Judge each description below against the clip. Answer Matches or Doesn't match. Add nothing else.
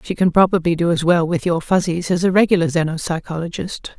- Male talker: Doesn't match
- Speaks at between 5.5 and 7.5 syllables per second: Matches